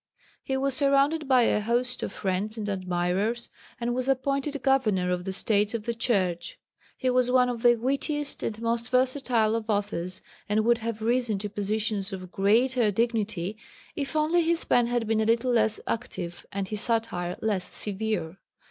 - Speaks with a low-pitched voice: No, high, 225 Hz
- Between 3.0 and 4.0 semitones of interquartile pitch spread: Yes, average, 3.7 semitones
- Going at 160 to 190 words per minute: Yes, average, 175 wpm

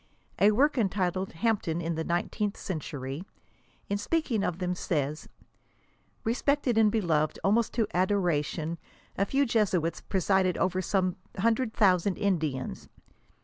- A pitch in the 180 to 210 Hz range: Yes, high, 190 Hz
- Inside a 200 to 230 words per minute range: No, slow, 135 wpm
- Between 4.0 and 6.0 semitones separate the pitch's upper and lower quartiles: Yes, average, 4.3 semitones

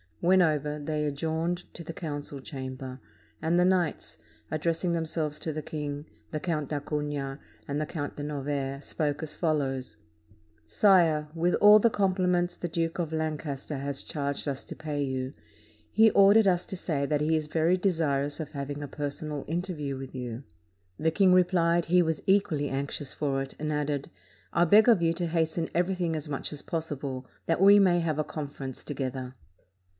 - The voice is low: No, medium, 155 Hz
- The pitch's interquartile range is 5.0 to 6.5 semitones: No, average, 3.2 semitones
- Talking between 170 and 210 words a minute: Yes, average, 180 wpm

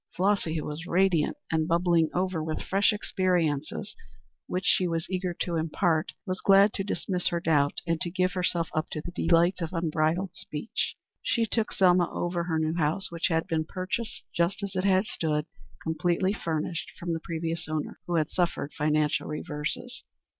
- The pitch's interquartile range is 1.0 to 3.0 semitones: Yes, narrow, 2.6 semitones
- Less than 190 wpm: Yes, average, 175 wpm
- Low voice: No, medium, 170 Hz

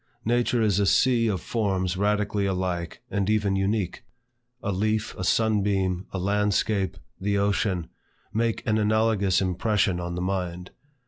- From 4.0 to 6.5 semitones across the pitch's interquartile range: No, narrow, 2.5 semitones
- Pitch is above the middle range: No, low, 100 Hz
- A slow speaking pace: No, average, 145 wpm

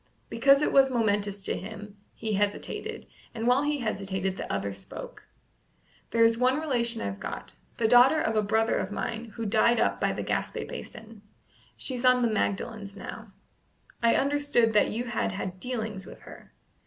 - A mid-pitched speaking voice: No, high, 225 Hz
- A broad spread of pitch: No, average, 3.4 semitones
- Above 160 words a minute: Yes, average, 170 wpm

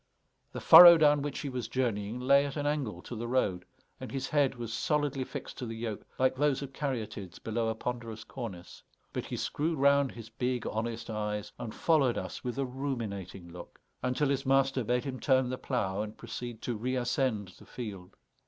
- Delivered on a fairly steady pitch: No, average, 3.6 semitones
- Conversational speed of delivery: Yes, average, 195 wpm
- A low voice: Yes, low, 125 Hz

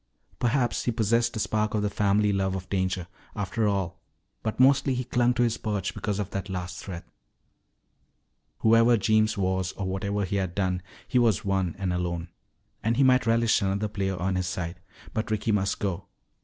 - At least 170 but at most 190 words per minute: Yes, average, 185 wpm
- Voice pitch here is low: Yes, low, 100 Hz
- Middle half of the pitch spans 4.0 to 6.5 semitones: No, average, 3.4 semitones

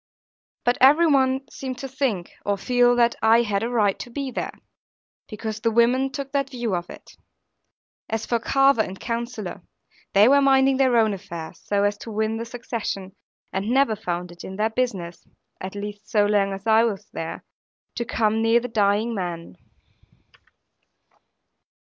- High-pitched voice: Yes, high, 225 Hz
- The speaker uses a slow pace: No, average, 170 wpm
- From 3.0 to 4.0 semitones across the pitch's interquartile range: Yes, average, 3.5 semitones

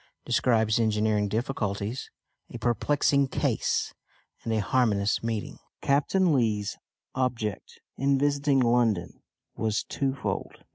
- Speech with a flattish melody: No, average, 4.1 semitones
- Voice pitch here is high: No, low, 115 Hz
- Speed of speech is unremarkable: No, slow, 100 wpm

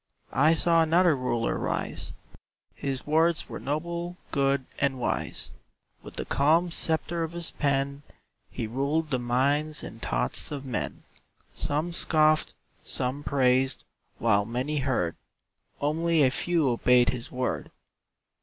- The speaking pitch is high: No, medium, 140 Hz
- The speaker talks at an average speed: No, slow, 130 wpm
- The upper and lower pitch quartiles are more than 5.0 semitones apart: No, average, 4.0 semitones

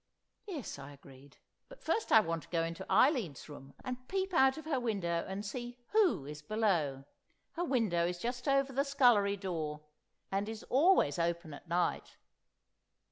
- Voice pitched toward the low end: No, high, 200 Hz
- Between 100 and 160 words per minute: No, average, 170 wpm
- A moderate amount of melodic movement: No, wide, 8.1 semitones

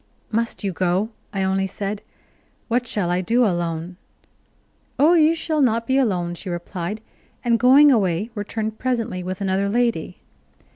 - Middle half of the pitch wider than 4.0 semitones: Yes, average, 4.7 semitones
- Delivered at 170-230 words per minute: No, average, 150 wpm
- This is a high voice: Yes, high, 210 Hz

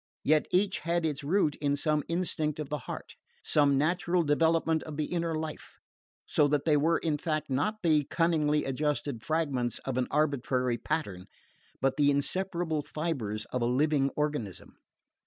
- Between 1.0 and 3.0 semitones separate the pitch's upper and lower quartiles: Yes, narrow, 2.6 semitones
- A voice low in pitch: No, medium, 150 Hz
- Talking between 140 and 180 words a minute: Yes, average, 160 wpm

